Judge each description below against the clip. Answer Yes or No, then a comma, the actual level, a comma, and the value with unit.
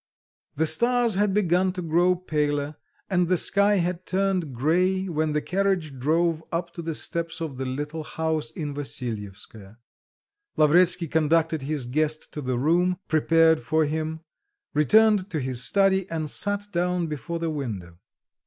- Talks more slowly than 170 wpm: Yes, average, 155 wpm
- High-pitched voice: No, medium, 160 Hz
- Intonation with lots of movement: No, average, 3.5 semitones